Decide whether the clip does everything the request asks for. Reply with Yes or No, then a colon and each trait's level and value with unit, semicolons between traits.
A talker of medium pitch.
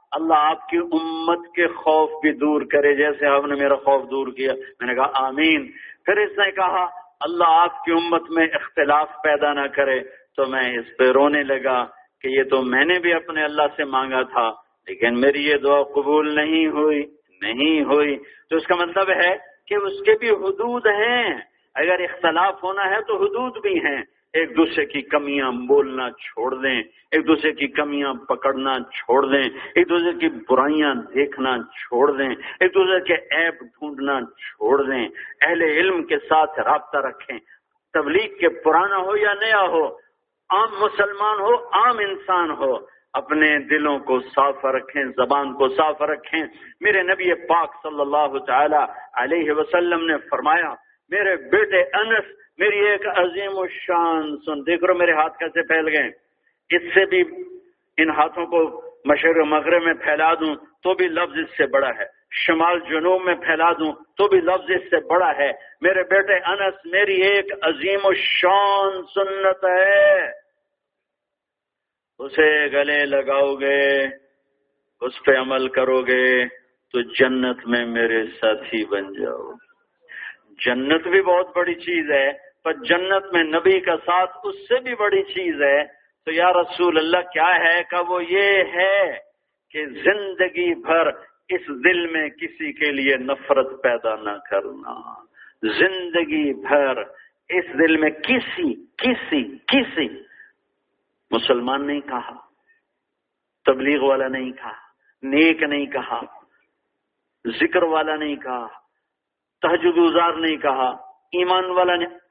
Yes: medium, 165 Hz